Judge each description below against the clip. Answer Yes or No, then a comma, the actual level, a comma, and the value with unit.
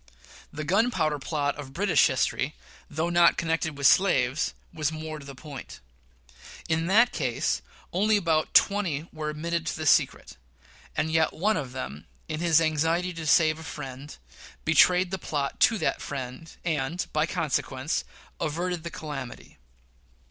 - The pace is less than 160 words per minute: Yes, average, 150 wpm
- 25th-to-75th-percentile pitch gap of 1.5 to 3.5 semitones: Yes, average, 2.9 semitones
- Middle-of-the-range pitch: Yes, medium, 155 Hz